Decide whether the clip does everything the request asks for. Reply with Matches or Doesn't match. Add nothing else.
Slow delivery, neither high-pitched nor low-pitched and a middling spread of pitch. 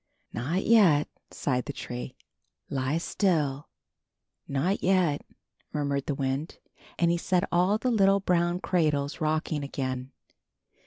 Matches